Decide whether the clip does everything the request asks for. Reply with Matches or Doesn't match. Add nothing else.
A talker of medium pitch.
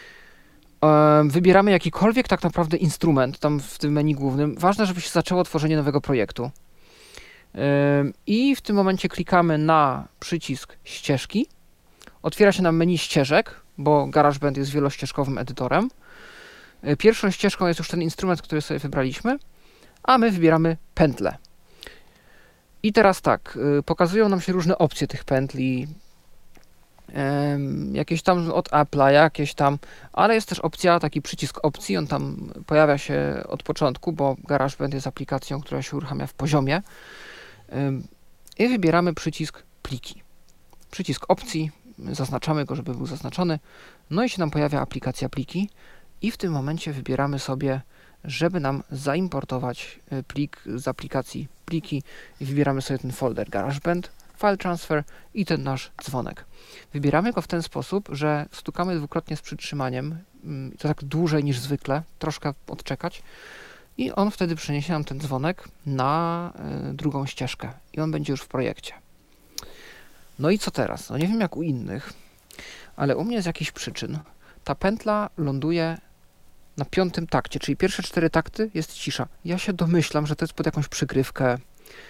Matches